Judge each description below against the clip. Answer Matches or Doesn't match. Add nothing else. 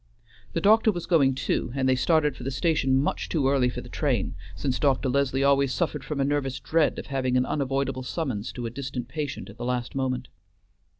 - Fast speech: Matches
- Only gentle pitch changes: Matches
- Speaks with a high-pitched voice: Doesn't match